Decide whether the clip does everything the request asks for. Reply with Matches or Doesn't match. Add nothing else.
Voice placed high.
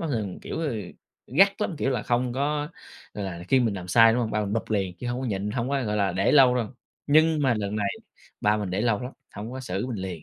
Doesn't match